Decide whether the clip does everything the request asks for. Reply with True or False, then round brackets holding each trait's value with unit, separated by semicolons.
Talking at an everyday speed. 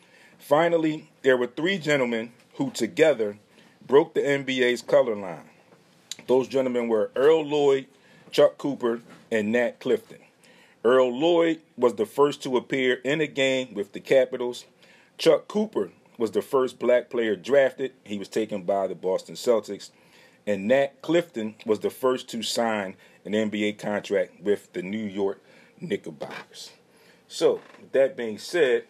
True (145 wpm)